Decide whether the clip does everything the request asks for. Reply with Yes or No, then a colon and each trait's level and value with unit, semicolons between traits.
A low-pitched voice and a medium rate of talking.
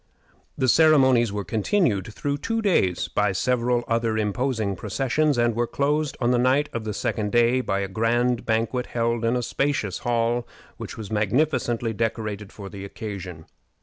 Yes: low, 115 Hz; average, 165 wpm